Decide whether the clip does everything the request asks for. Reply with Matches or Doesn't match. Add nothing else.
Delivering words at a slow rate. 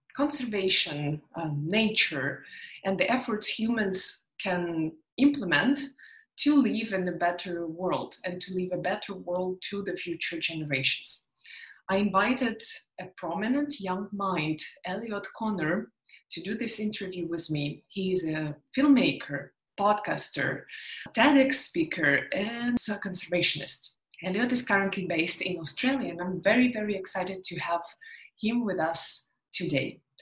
Matches